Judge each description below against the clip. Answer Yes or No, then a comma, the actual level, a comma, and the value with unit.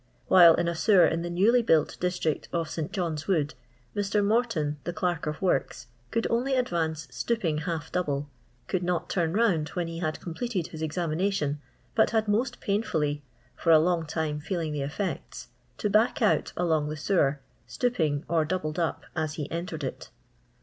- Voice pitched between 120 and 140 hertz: No, medium, 170 Hz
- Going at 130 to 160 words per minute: No, average, 175 wpm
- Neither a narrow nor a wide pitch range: Yes, average, 4.1 semitones